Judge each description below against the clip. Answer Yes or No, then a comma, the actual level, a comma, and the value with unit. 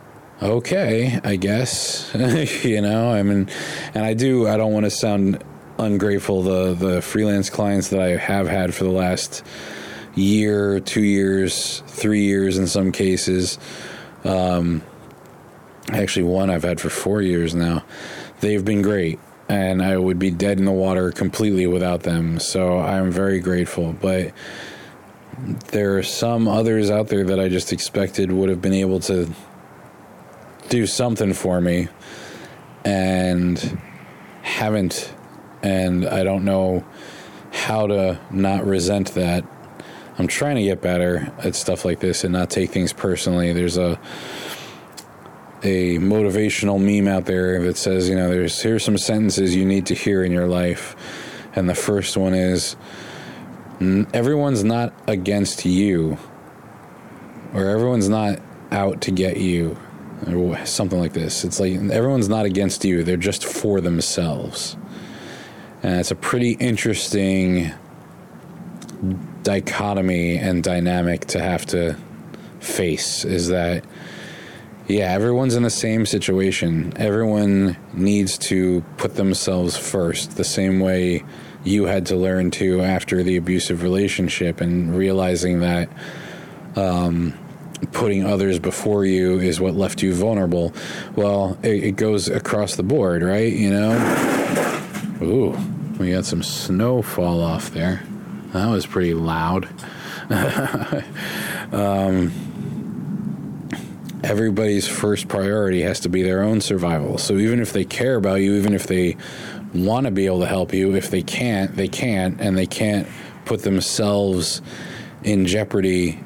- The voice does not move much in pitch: Yes, narrow, 2.1 semitones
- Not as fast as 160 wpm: Yes, average, 140 wpm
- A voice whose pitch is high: No, very low, 95 Hz